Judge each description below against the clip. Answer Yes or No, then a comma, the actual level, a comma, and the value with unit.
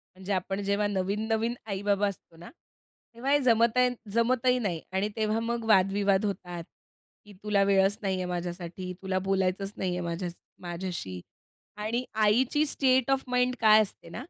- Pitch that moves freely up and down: No, average, 3.5 semitones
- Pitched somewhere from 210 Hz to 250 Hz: No, high, 200 Hz